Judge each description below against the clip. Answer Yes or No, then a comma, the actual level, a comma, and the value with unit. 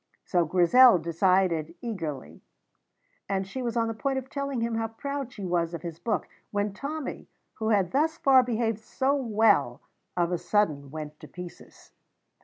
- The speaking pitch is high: Yes, high, 210 Hz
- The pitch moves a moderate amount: No, wide, 6.3 semitones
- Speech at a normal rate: Yes, average, 170 wpm